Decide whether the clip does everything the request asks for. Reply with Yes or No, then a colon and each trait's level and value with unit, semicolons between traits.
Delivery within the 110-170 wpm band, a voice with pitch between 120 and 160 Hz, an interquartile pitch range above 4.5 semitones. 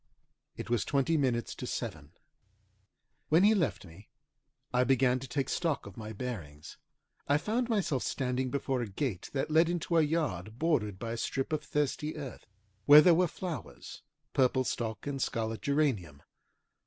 Yes: average, 165 wpm; low, 135 Hz; average, 5.3 semitones